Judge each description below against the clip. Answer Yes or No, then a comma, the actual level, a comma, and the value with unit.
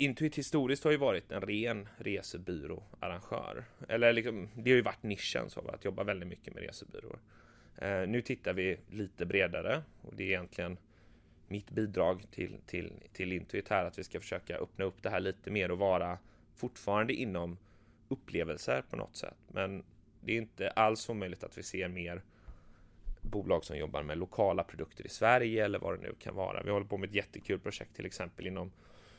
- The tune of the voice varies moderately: Yes, average, 3.3 semitones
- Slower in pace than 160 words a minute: No, average, 190 wpm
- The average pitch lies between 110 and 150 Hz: No, low, 100 Hz